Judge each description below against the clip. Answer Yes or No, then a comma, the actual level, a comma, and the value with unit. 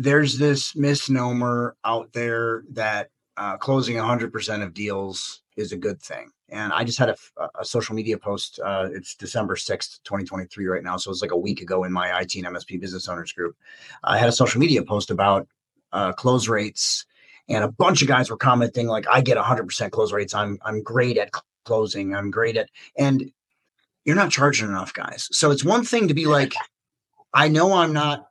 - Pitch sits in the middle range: No, low, 115 Hz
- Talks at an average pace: Yes, average, 195 wpm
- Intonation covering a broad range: Yes, wide, 5.7 semitones